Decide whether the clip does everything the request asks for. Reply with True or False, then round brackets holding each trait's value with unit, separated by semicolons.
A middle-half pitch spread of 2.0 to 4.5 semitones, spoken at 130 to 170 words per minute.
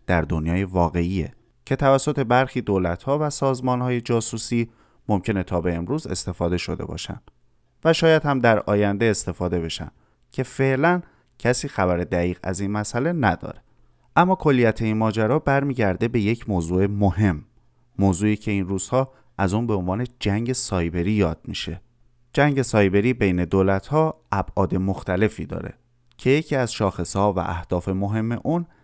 False (5.2 semitones; 145 wpm)